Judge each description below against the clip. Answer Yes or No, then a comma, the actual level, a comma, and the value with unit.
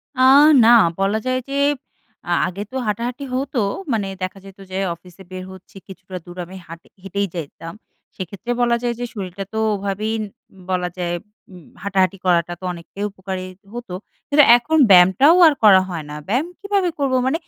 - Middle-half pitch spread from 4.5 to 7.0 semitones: Yes, average, 4.9 semitones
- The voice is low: No, high, 195 Hz